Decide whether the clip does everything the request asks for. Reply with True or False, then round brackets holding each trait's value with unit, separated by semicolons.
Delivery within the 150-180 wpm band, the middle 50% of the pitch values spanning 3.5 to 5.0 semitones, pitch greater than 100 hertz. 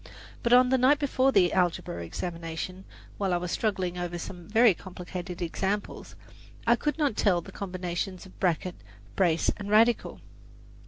True (155 wpm; 4.2 semitones; 185 Hz)